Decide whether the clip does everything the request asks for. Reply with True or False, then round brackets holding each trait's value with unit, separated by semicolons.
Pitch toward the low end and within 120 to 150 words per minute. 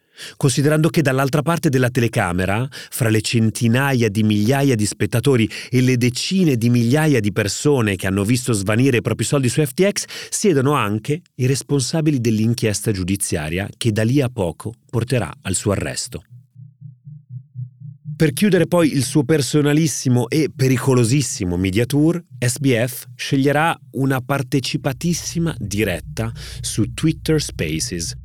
True (130 Hz; 130 wpm)